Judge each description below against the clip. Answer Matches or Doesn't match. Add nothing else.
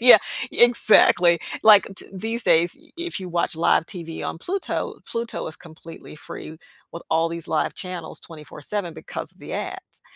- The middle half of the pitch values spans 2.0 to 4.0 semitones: Doesn't match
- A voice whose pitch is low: Doesn't match